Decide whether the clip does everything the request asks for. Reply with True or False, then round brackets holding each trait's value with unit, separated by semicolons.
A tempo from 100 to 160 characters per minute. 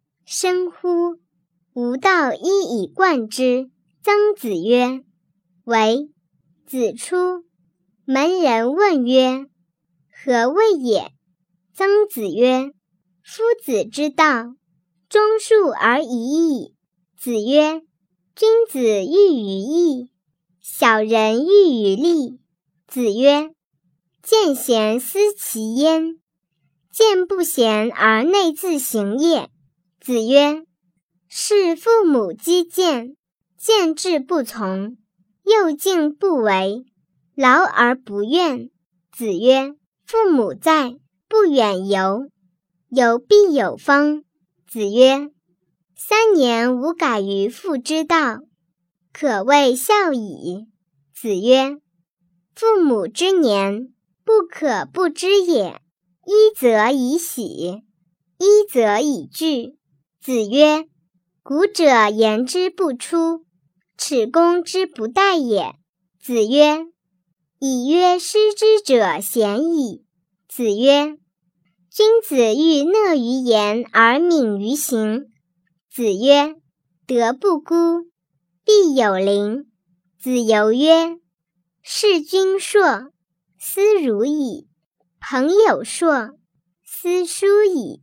True (125 characters per minute)